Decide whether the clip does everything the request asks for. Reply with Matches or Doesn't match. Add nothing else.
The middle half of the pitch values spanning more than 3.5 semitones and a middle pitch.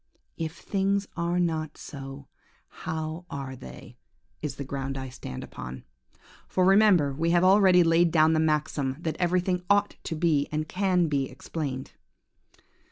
Matches